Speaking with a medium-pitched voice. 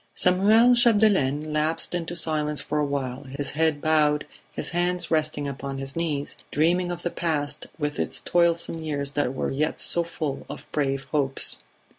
Yes: medium, 155 Hz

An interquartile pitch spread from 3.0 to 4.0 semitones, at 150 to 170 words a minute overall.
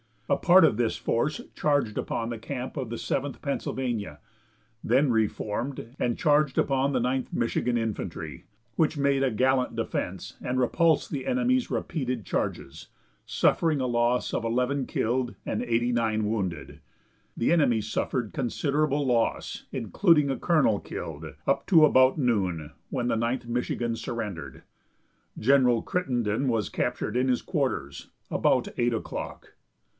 No: average, 3.5 semitones; average, 140 wpm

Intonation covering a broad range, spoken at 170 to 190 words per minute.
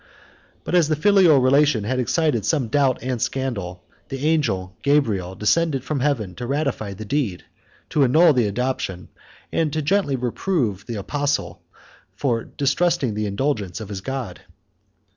No: wide, 5.8 semitones; average, 150 wpm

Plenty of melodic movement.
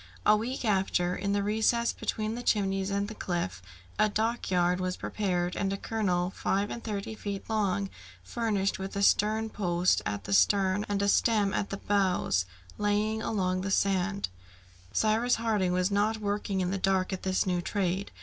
No: narrow, 2.4 semitones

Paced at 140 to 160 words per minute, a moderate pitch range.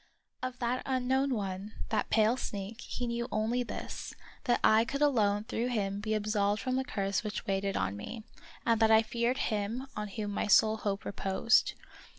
No: average, 180 wpm; average, 3.1 semitones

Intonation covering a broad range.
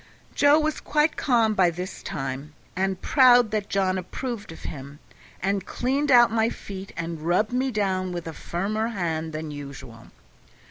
Yes: wide, 6.2 semitones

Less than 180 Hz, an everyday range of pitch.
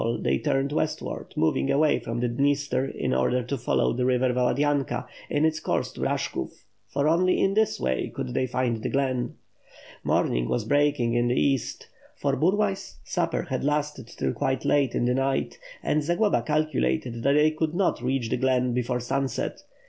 Yes: low, 135 Hz; average, 3.4 semitones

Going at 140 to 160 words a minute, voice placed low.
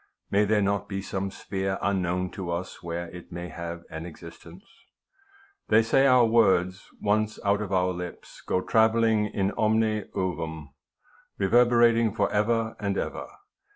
Yes: average, 150 wpm; low, 100 Hz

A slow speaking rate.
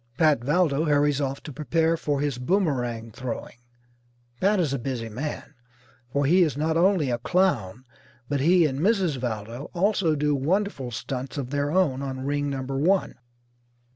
No: average, 165 wpm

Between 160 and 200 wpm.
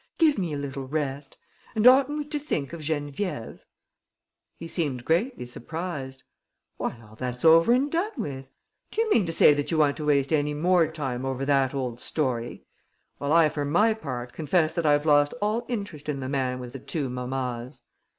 Yes: average, 190 wpm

